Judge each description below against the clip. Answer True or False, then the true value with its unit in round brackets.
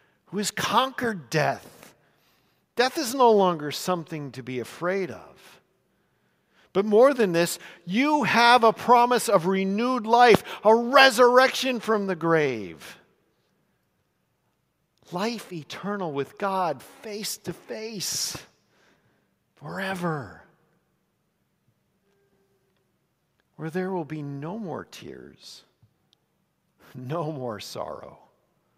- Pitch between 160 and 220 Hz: True (190 Hz)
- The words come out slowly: True (100 wpm)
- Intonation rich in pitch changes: True (6.4 semitones)